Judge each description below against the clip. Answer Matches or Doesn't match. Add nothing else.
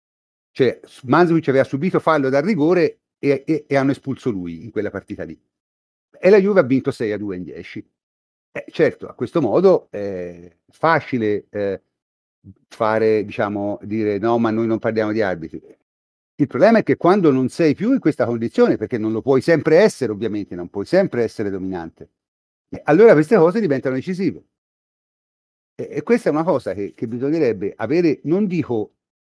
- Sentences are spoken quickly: Matches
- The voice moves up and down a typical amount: Doesn't match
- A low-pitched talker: Matches